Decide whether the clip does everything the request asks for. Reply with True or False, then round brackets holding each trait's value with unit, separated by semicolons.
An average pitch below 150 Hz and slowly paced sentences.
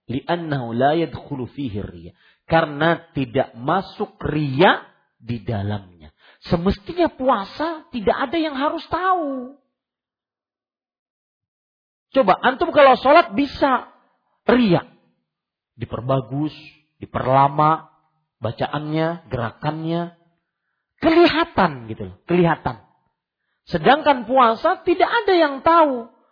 False (170 Hz; 75 wpm)